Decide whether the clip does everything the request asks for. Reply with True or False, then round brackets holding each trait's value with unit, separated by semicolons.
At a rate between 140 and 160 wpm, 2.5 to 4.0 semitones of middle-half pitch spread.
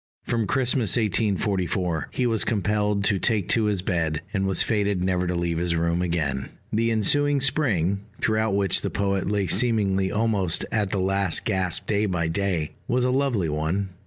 False (175 wpm; 3.5 semitones)